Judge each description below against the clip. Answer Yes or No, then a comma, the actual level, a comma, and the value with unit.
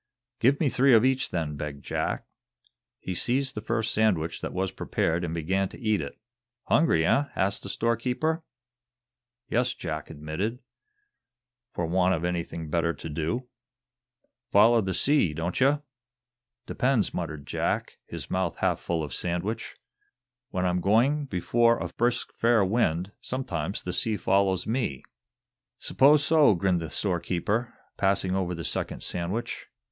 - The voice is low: Yes, very low, 95 Hz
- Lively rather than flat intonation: Yes, wide, 5.9 semitones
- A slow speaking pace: No, average, 145 wpm